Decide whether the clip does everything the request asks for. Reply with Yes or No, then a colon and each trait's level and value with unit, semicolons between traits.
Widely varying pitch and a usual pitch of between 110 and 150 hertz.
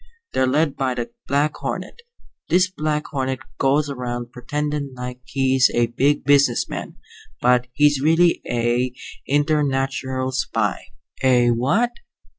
No: average, 2.8 semitones; low, 135 Hz